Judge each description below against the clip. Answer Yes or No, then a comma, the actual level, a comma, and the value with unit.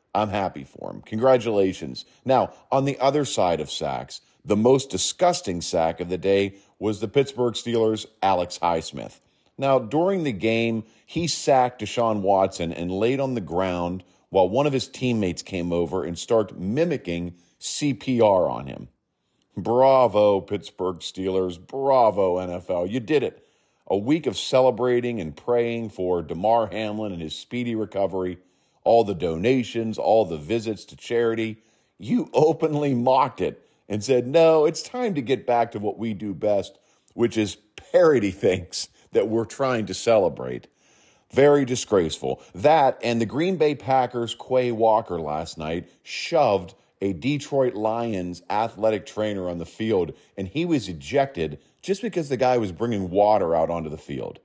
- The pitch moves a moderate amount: No, wide, 5.7 semitones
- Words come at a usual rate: Yes, average, 155 wpm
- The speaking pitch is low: Yes, low, 110 Hz